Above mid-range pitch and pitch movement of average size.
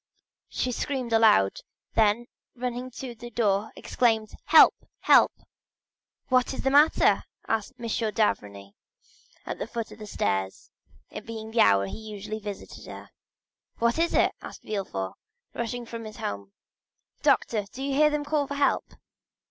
Yes: high, 225 Hz; average, 3.4 semitones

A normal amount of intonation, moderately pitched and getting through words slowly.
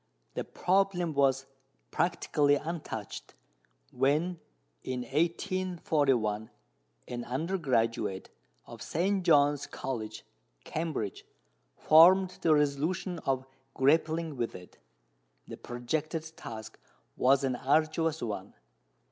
Yes: average, 5.0 semitones; medium, 145 Hz; slow, 90 wpm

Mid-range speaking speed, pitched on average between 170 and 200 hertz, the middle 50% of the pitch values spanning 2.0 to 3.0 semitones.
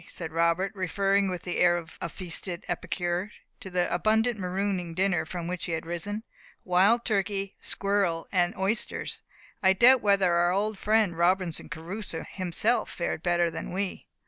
Yes: average, 160 wpm; medium, 185 Hz; narrow, 2.6 semitones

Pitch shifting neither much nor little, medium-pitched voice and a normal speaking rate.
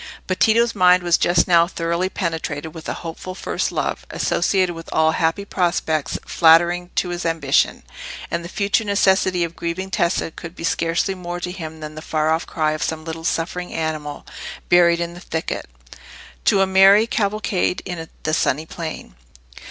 No: narrow, 2.3 semitones; medium, 170 Hz; average, 175 wpm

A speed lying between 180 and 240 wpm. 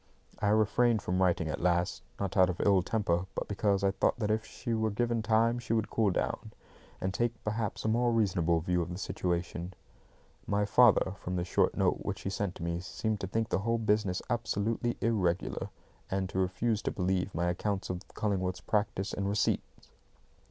Yes: average, 190 wpm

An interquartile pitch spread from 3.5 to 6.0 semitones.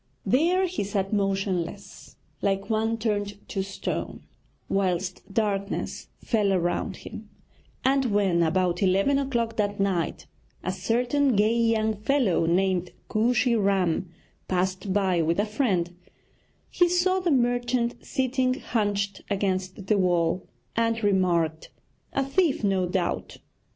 Yes: average, 4.1 semitones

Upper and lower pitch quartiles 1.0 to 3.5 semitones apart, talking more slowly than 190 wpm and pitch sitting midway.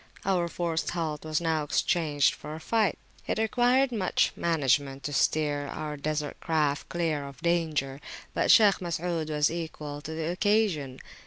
Yes: average, 2.9 semitones; average, 155 wpm; medium, 160 Hz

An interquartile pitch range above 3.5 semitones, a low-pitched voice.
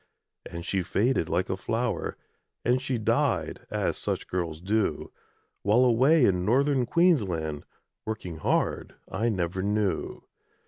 Yes: wide, 5.5 semitones; low, 105 Hz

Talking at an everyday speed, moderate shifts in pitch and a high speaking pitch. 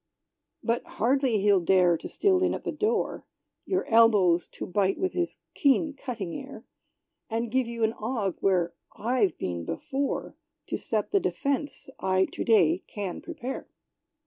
No: average, 155 wpm; wide, 6.2 semitones; high, 230 Hz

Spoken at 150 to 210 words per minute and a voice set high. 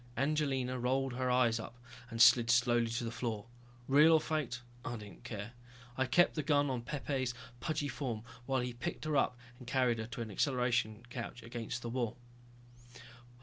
No: average, 180 wpm; low, 125 Hz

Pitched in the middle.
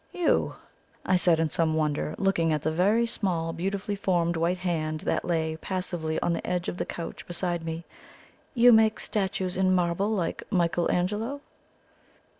Yes: medium, 175 Hz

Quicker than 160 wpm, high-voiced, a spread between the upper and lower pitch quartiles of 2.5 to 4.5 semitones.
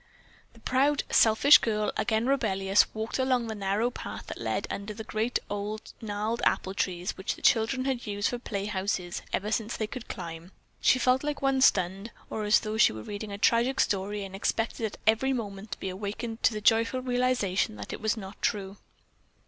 Yes: average, 195 wpm; high, 215 Hz; average, 3.1 semitones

